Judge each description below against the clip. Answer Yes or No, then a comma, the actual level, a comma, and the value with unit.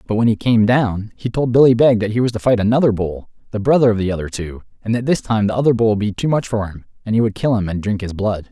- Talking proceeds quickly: Yes, fast, 305 wpm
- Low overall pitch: Yes, low, 110 Hz